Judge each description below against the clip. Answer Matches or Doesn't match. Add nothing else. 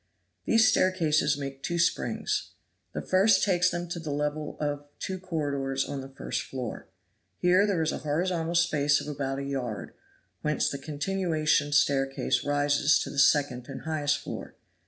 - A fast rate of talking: Doesn't match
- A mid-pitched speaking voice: Matches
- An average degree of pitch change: Matches